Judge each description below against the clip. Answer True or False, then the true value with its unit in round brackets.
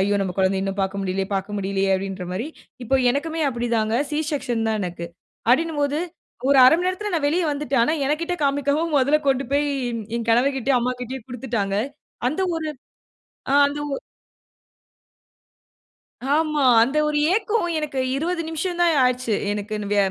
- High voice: True (265 Hz)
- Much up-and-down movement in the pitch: True (6.4 semitones)